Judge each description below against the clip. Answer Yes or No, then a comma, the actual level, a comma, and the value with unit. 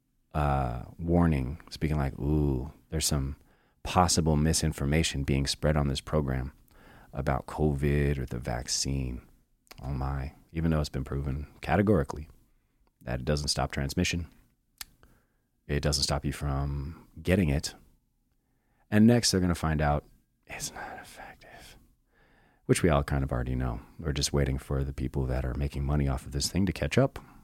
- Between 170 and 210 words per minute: No, average, 160 wpm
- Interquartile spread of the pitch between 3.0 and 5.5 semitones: No, narrow, 2.4 semitones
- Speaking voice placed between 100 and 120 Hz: No, very low, 70 Hz